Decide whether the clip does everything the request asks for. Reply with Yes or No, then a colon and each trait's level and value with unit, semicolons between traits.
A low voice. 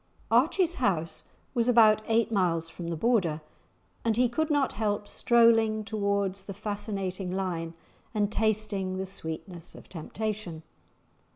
No: high, 205 Hz